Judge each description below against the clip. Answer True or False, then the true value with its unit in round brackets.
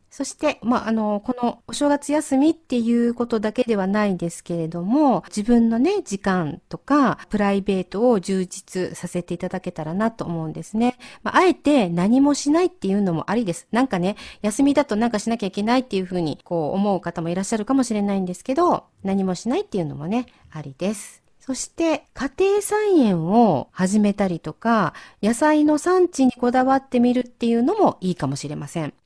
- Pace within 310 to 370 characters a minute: False (395 characters per minute)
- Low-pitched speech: False (220 Hz)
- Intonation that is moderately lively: False (6.1 semitones)